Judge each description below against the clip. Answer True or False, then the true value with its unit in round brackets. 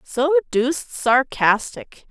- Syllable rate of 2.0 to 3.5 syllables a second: True (3.2 syllables/s)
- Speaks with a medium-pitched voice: False (240 Hz)